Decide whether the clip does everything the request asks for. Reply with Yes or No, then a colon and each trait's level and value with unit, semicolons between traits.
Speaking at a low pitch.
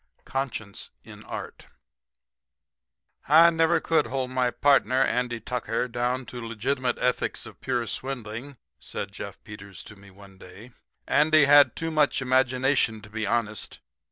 Yes: low, 125 Hz